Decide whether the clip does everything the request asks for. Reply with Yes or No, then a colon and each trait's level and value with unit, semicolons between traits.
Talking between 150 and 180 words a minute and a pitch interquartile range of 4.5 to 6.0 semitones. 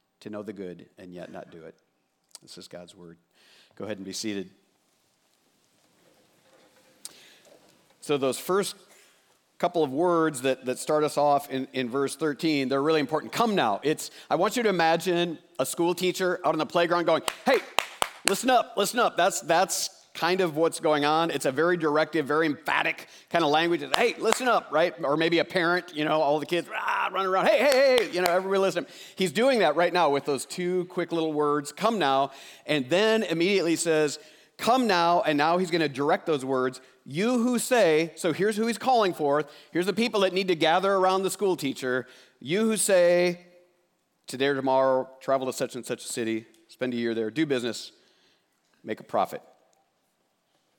No: average, 195 wpm; average, 4.8 semitones